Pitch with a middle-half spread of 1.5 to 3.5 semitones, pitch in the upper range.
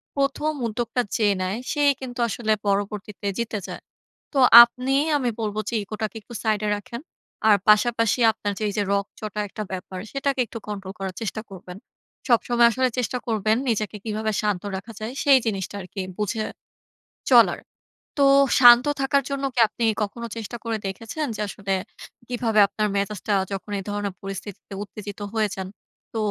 Yes: average, 2.8 semitones; high, 215 Hz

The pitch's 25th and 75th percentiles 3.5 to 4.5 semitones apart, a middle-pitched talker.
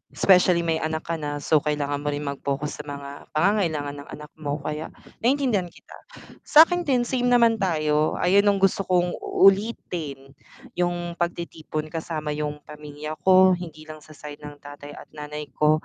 Yes: average, 3.9 semitones; medium, 155 Hz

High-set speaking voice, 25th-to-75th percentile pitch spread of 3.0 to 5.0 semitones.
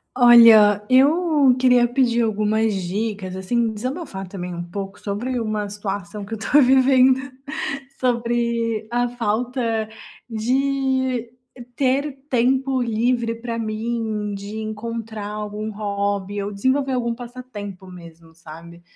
Yes: high, 225 Hz; average, 3.4 semitones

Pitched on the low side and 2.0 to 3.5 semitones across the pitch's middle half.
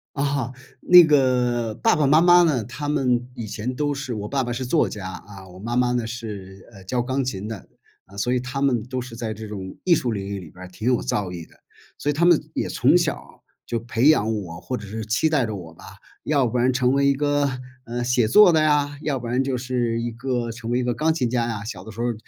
No: low, 120 Hz; average, 3.9 semitones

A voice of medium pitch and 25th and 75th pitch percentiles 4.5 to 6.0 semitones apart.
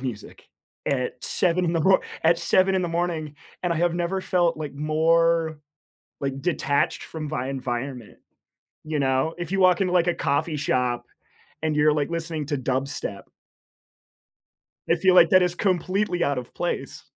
No: medium, 160 Hz; average, 3.7 semitones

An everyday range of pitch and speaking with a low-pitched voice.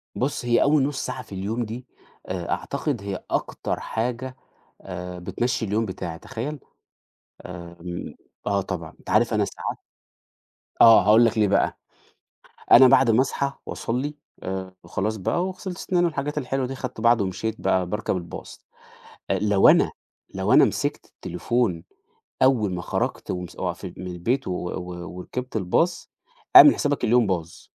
No: wide, 5.8 semitones; low, 110 Hz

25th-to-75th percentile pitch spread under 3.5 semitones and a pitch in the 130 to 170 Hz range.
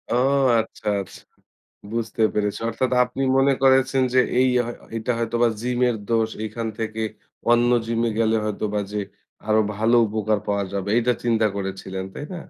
No: narrow, 2.4 semitones; low, 115 Hz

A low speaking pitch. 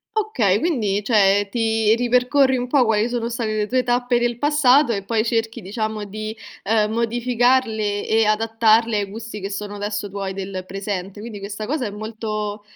No: high, 220 Hz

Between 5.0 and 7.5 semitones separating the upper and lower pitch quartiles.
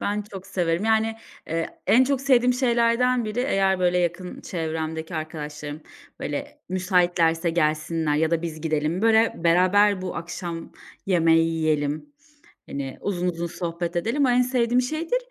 Yes: wide, 5.5 semitones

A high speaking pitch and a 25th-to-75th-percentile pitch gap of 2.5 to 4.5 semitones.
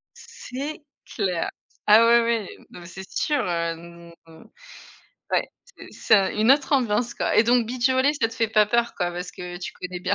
No: high, 220 Hz; wide, 5.6 semitones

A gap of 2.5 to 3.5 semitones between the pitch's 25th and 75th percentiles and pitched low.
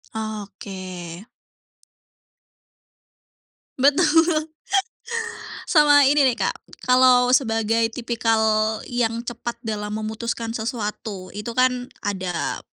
No: average, 3.2 semitones; high, 230 Hz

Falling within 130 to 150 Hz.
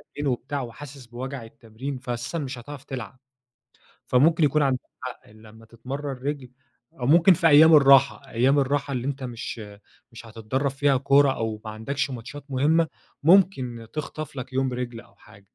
Yes: low, 135 Hz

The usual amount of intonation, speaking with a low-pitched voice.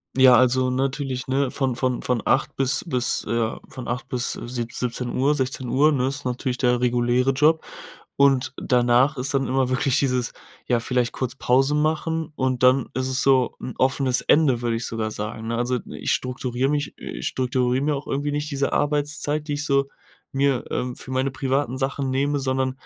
No: narrow, 1.9 semitones; low, 130 Hz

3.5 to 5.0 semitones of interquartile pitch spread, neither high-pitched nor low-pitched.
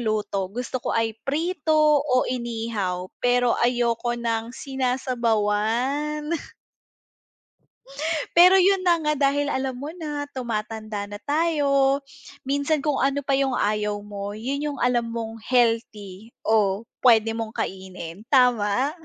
No: average, 4.3 semitones; high, 240 Hz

